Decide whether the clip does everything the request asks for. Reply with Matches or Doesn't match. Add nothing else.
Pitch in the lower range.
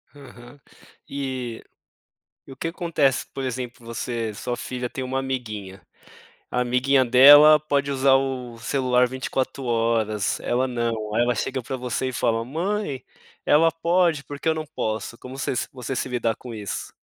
Matches